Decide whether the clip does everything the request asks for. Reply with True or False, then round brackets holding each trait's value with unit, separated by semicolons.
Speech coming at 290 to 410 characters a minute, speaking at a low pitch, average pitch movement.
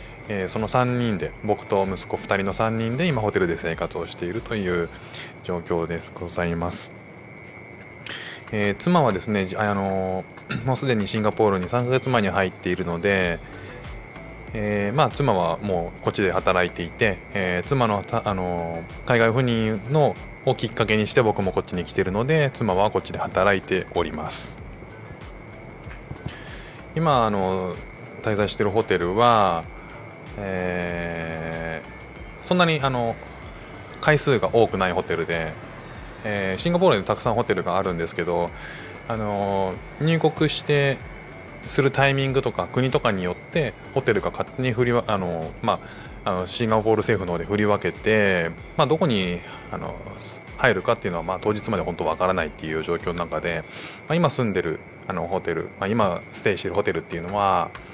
True (320 characters per minute; 100 Hz; 5.0 semitones)